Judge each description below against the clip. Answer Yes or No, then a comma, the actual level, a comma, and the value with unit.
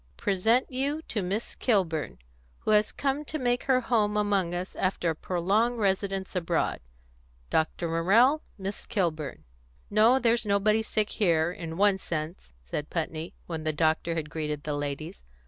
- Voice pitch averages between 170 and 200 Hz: Yes, high, 190 Hz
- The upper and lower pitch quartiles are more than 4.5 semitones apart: Yes, average, 5.2 semitones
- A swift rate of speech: No, average, 155 wpm